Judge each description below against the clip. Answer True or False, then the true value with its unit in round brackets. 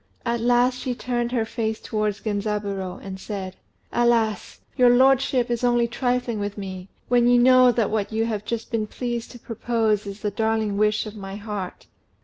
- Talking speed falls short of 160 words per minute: False (180 wpm)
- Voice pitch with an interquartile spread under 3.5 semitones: True (2.7 semitones)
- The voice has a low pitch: False (225 Hz)